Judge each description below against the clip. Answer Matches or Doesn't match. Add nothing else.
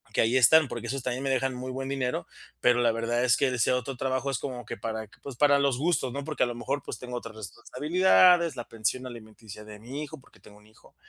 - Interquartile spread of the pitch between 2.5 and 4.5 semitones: Matches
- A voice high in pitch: Doesn't match